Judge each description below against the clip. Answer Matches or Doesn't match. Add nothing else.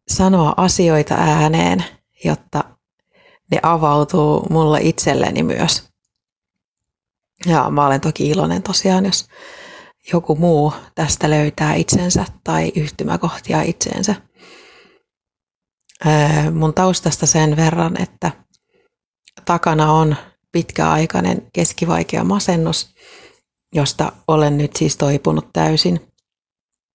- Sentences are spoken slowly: Matches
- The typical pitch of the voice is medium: Matches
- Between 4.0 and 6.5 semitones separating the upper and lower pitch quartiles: Doesn't match